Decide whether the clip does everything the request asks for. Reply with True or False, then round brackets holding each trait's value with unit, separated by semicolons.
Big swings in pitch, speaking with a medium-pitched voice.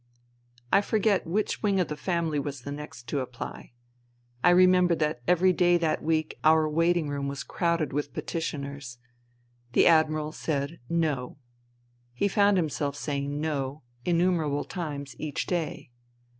False (3.5 semitones; 155 Hz)